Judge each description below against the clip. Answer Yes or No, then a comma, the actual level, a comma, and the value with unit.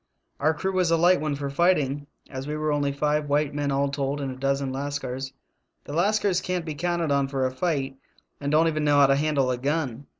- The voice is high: No, medium, 145 Hz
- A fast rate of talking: Yes, fast, 230 wpm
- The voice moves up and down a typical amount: No, narrow, 2.3 semitones